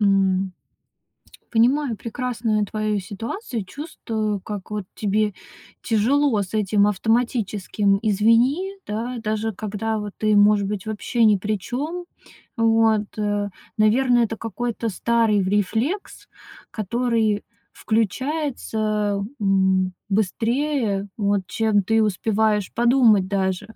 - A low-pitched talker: No, high, 215 Hz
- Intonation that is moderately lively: No, narrow, 2.3 semitones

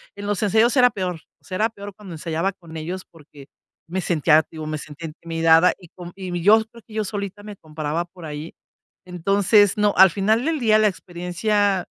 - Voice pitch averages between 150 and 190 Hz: Yes, medium, 185 Hz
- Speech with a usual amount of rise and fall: Yes, average, 4.0 semitones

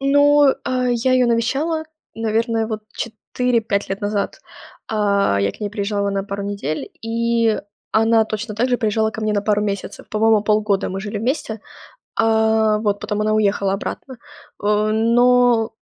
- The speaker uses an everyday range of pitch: No, narrow, 2.2 semitones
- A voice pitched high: Yes, high, 220 Hz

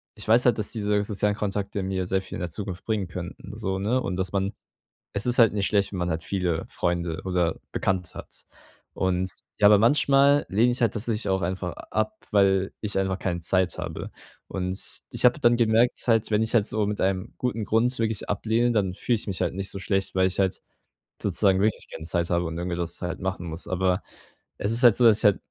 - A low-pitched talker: Yes, low, 100 Hz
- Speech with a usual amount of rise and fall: Yes, average, 3.0 semitones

